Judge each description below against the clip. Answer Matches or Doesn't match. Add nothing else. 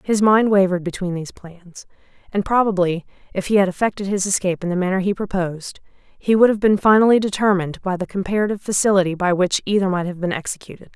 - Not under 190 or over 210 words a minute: Matches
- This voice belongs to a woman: Matches